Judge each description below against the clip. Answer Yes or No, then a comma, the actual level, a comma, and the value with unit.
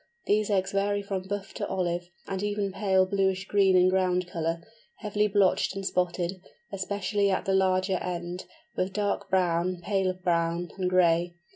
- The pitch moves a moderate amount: No, narrow, 1.7 semitones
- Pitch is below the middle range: No, medium, 185 Hz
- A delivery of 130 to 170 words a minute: Yes, average, 160 wpm